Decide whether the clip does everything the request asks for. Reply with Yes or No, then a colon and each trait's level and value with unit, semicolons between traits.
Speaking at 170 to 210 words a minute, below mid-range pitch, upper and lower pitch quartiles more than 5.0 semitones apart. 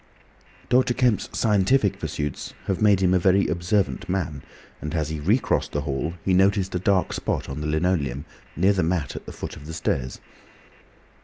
No: average, 180 wpm; very low, 90 Hz; average, 4.4 semitones